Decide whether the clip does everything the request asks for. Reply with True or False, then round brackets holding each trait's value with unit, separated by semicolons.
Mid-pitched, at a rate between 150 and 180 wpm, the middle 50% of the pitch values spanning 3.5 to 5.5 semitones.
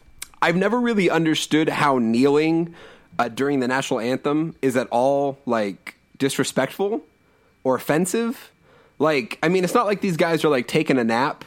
True (150 Hz; 160 wpm; 4.6 semitones)